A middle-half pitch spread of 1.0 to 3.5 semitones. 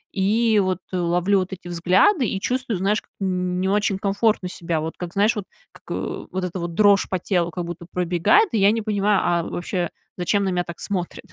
Yes: narrow, 2.5 semitones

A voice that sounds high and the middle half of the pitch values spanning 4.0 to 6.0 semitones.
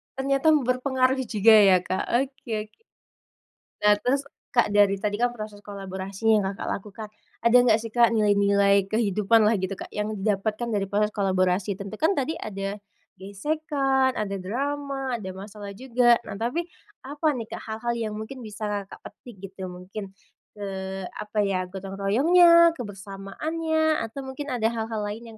Yes: high, 215 Hz; average, 4.6 semitones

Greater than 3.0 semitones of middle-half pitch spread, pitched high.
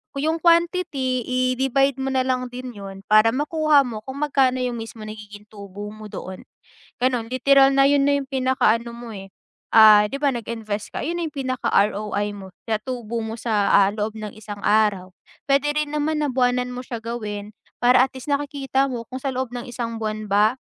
Yes: average, 4.1 semitones; high, 245 Hz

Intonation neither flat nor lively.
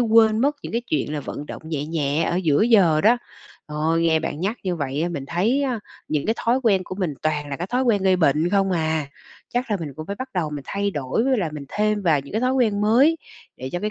No: wide, 6.2 semitones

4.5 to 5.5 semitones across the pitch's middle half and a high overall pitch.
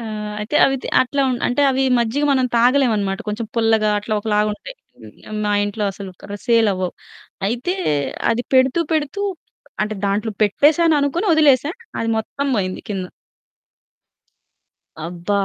Yes: average, 4.9 semitones; high, 230 Hz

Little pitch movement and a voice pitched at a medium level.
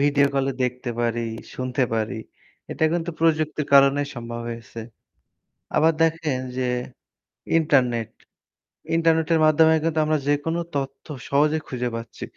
No: average, 4.1 semitones; medium, 145 Hz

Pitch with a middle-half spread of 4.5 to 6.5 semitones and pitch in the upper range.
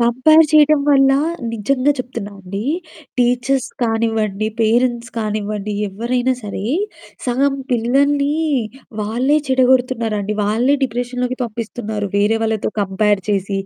No: average, 3.4 semitones; high, 235 Hz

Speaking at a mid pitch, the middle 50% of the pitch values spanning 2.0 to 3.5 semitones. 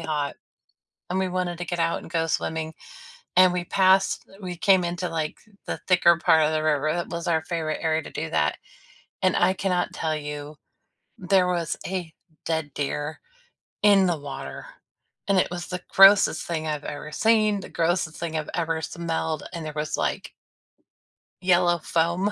Yes: medium, 170 Hz; narrow, 2.5 semitones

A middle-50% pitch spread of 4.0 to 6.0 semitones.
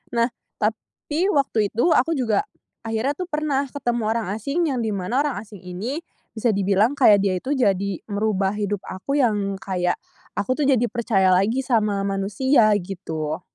Yes: average, 5.0 semitones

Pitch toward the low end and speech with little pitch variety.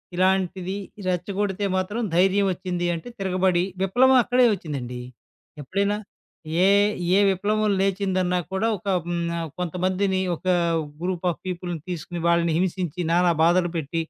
No: medium, 185 Hz; narrow, 2.0 semitones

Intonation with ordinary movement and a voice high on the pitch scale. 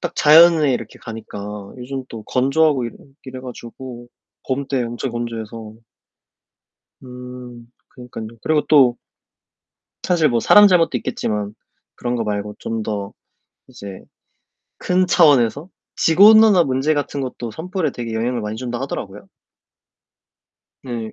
No: average, 4.4 semitones; low, 125 Hz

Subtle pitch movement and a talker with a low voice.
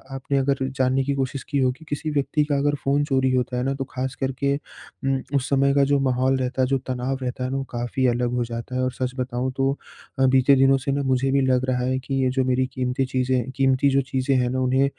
Yes: narrow, 1.2 semitones; low, 130 Hz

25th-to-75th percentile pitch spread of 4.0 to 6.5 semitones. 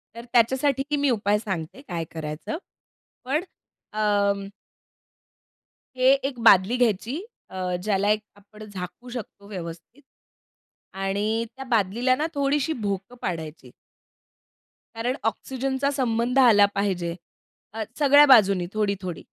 Yes: average, 4.9 semitones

